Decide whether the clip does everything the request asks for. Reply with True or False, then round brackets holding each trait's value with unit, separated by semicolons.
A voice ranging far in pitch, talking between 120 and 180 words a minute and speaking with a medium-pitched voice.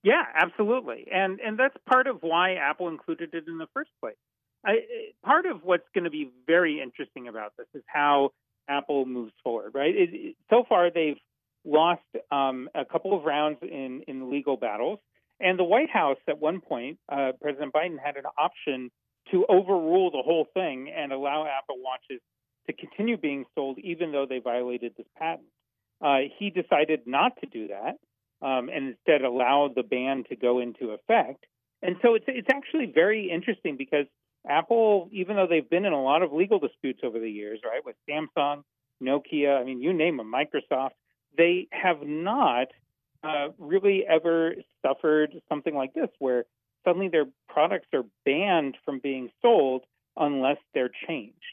True (5.7 semitones; 175 wpm; 150 Hz)